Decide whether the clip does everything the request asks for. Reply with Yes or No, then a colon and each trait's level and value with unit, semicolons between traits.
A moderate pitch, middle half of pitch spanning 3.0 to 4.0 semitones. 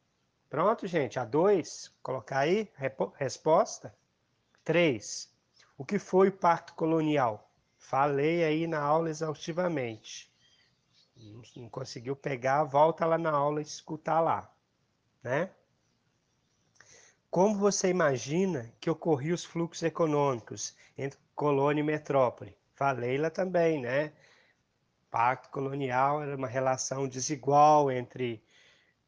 Yes: medium, 150 Hz; average, 3.5 semitones